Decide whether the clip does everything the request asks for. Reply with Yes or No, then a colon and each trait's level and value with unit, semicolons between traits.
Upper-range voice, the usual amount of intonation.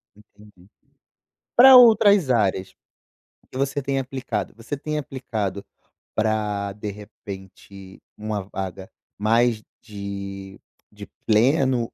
No: low, 105 Hz; average, 4.7 semitones